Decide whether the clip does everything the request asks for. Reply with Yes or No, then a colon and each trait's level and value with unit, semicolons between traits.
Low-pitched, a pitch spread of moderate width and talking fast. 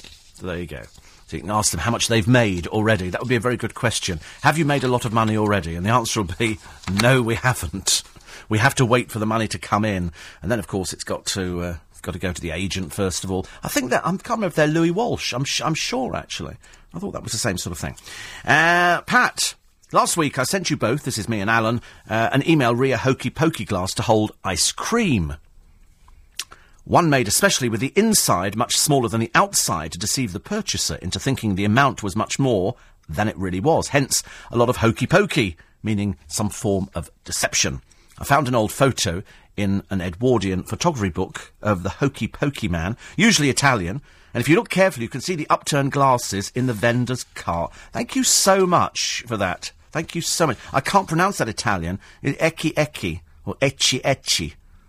No: low, 115 Hz; wide, 6.7 semitones; fast, 220 wpm